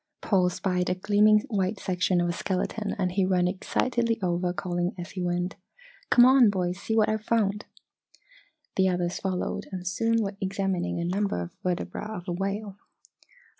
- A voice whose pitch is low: No, high, 190 Hz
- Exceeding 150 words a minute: Yes, average, 170 wpm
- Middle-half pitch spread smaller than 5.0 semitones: Yes, average, 2.7 semitones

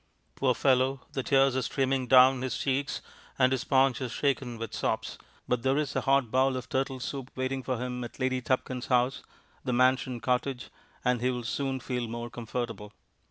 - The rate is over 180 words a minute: Yes, average, 190 wpm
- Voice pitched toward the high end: No, low, 130 Hz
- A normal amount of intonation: No, narrow, 1.4 semitones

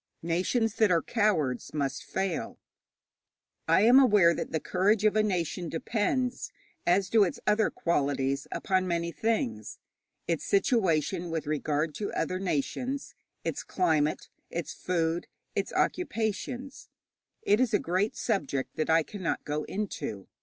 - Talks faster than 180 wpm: No, average, 140 wpm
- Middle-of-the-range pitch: Yes, medium, 180 Hz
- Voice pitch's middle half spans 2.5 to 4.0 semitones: No, average, 5.1 semitones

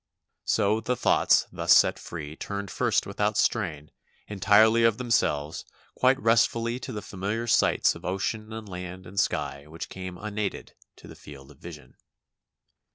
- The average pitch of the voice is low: Yes, low, 100 Hz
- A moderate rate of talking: Yes, average, 155 wpm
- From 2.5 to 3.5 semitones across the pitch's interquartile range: No, average, 5.0 semitones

